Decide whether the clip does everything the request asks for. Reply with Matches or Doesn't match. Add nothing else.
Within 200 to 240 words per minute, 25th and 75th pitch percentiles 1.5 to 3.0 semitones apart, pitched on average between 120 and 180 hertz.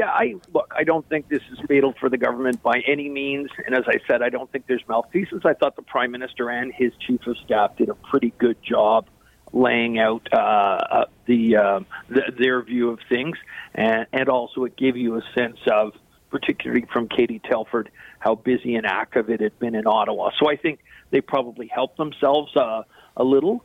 Matches